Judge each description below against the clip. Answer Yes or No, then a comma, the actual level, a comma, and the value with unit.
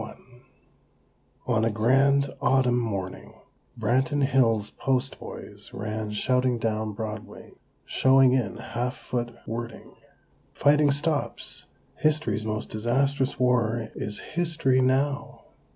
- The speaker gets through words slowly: Yes, slow, 105 wpm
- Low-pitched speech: Yes, low, 125 Hz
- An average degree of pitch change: Yes, average, 3.4 semitones